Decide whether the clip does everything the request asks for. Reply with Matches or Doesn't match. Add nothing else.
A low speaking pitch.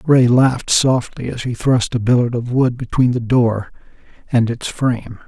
Matches